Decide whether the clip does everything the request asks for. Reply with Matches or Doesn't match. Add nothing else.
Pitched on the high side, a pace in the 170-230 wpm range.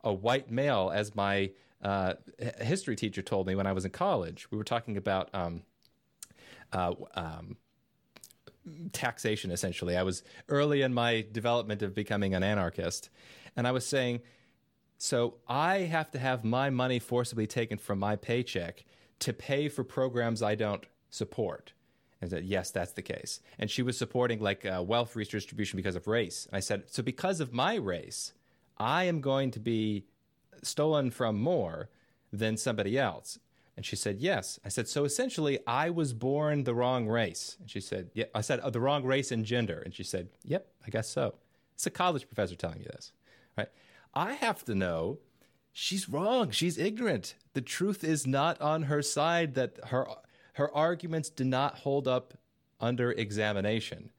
Doesn't match